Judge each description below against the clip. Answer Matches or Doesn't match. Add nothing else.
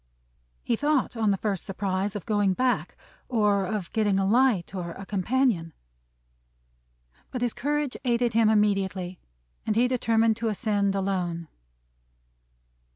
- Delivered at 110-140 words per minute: Matches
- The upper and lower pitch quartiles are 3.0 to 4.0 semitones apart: Matches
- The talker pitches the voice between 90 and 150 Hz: Doesn't match